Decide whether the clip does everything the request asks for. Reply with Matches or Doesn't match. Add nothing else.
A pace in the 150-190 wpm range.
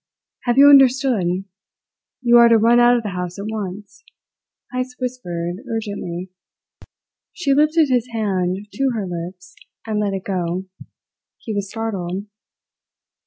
Doesn't match